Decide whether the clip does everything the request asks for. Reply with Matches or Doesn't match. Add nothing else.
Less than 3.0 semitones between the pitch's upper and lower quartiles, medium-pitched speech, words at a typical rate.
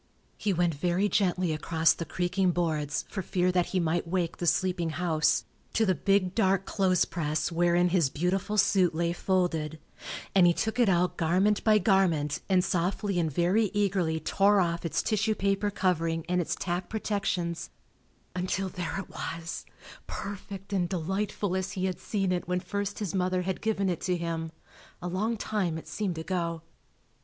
Matches